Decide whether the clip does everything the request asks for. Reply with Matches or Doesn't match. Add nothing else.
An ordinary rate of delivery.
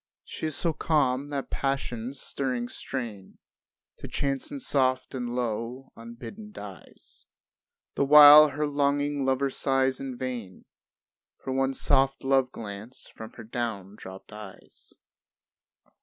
Doesn't match